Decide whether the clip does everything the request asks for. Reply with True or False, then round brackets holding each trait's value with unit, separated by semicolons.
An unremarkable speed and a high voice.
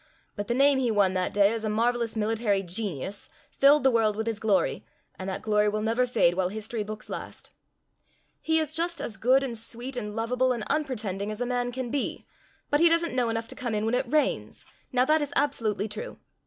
False (220 wpm; 230 Hz)